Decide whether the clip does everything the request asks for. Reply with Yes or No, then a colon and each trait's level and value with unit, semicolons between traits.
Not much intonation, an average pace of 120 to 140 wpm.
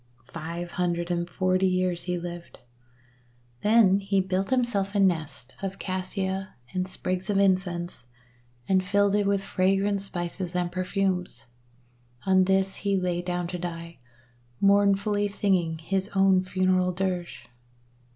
Yes: narrow, 1.8 semitones; slow, 135 wpm